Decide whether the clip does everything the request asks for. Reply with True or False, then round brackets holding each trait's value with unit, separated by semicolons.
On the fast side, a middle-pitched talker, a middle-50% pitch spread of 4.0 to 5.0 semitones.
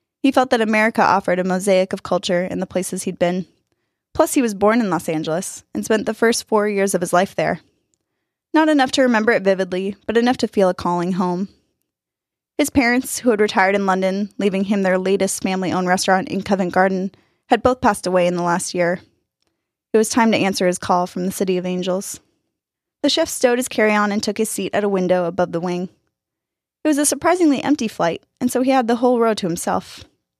False (215 wpm; 195 Hz; 4.4 semitones)